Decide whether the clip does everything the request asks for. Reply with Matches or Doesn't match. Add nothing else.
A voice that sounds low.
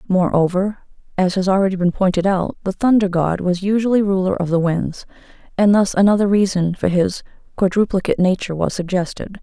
Doesn't match